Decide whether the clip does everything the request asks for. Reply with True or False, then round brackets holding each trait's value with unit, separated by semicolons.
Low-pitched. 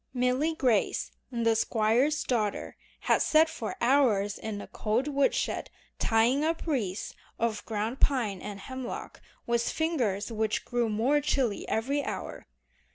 False (235 Hz)